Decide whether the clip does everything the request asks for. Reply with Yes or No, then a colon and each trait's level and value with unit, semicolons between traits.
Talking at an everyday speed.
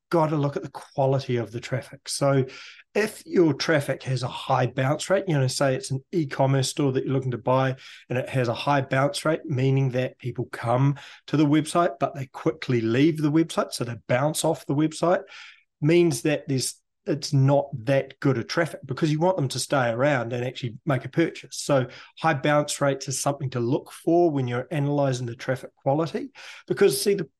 No: fast, 210 wpm